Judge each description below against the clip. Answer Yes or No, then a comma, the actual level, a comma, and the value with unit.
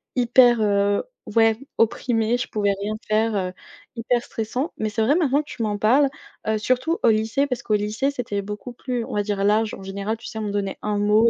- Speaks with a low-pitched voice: No, high, 220 Hz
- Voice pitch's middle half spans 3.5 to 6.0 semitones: No, average, 2.7 semitones